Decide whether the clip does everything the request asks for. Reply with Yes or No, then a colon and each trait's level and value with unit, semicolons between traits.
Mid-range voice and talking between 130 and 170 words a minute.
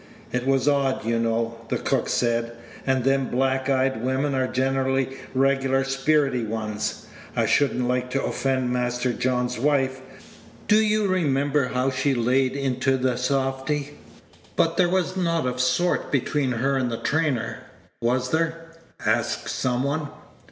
No: low, 130 Hz; average, 150 wpm